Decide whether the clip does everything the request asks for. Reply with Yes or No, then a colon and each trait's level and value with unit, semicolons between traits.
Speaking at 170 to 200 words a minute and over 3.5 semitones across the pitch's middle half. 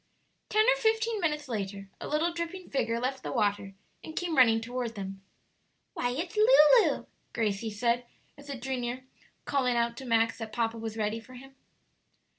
Yes: average, 175 wpm; average, 5.1 semitones